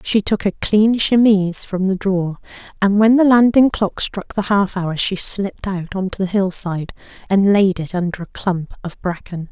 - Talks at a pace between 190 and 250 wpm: Yes, average, 200 wpm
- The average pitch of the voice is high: Yes, high, 195 Hz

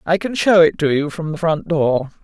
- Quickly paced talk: Yes, fast, 270 wpm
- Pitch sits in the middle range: Yes, medium, 160 Hz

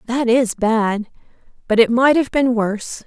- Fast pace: No, average, 175 wpm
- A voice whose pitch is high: Yes, high, 235 Hz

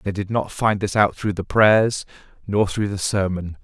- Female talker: No, male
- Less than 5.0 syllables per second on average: Yes, 4.5 syllables/s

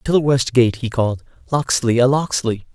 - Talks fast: No, average, 195 wpm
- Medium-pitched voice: No, low, 125 Hz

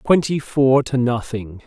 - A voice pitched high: No, low, 130 Hz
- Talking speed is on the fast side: No, average, 145 wpm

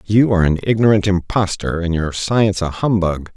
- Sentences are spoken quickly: No, average, 180 wpm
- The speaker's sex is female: No, male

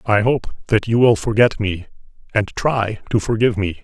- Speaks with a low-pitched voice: Yes, low, 110 Hz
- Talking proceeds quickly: No, average, 190 wpm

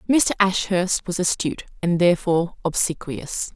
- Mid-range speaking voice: Yes, medium, 180 Hz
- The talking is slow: Yes, slow, 120 wpm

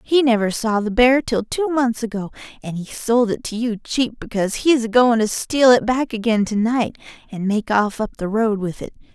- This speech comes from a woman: Yes, female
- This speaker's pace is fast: Yes, fast, 230 wpm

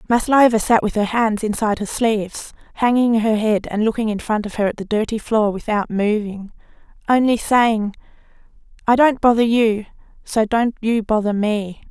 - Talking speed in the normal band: Yes, average, 170 wpm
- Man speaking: No, female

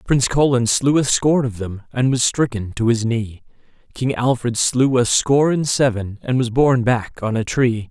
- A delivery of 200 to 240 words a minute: Yes, fast, 205 wpm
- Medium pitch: No, low, 120 Hz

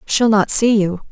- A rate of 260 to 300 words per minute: No, fast, 215 wpm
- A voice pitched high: Yes, high, 210 Hz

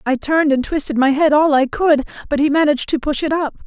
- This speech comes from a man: No, female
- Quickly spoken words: Yes, fast, 260 wpm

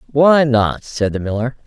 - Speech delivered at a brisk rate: No, average, 180 wpm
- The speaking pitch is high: No, low, 125 Hz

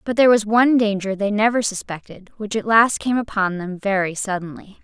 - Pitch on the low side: No, high, 210 Hz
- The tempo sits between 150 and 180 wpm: No, average, 200 wpm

